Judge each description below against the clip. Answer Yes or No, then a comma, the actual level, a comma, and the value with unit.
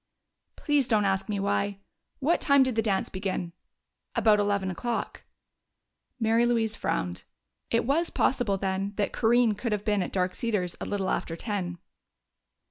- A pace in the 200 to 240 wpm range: No, average, 155 wpm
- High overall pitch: Yes, high, 210 Hz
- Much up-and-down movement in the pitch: No, average, 3.5 semitones